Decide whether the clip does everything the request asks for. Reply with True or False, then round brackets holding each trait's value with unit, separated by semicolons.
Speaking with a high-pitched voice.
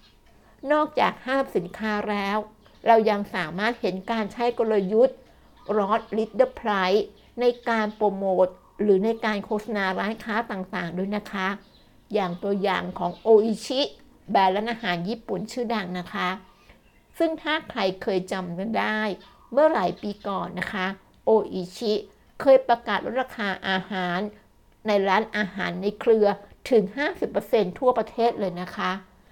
True (210 Hz)